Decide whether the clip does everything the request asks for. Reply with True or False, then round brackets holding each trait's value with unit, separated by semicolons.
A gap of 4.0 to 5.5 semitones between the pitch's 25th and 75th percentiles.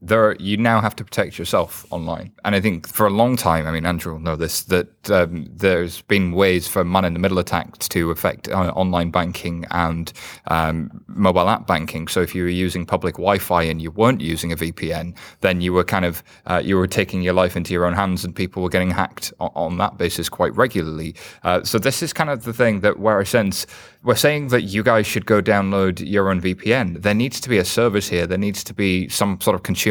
False (3.3 semitones)